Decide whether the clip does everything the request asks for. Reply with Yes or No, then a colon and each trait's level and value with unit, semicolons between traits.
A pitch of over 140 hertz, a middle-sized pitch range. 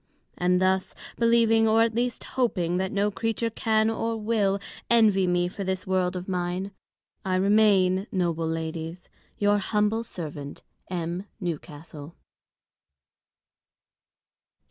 Yes: high, 190 Hz; average, 3.7 semitones